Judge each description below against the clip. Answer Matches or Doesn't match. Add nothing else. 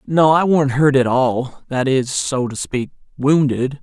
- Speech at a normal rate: Matches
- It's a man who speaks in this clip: Matches